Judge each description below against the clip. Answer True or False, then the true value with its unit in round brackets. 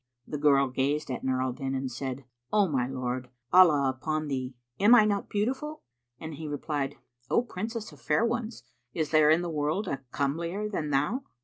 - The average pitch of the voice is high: False (150 Hz)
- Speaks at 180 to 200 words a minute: True (190 wpm)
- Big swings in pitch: True (7.0 semitones)